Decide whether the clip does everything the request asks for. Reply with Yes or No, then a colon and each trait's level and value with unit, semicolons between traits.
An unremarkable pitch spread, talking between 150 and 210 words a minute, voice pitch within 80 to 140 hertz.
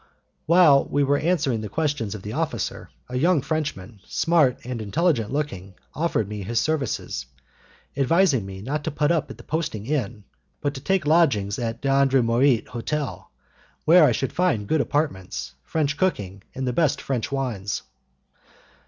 No: wide, 5.9 semitones; average, 160 wpm; low, 135 Hz